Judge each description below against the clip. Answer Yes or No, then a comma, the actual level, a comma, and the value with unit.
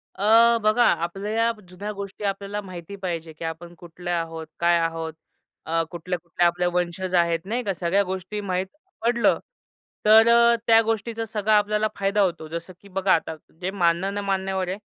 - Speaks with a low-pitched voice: No, high, 190 Hz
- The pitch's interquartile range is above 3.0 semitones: Yes, average, 3.4 semitones